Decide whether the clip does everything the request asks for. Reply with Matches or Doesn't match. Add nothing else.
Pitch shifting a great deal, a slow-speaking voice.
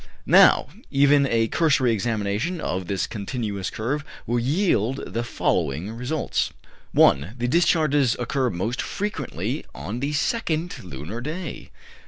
Matches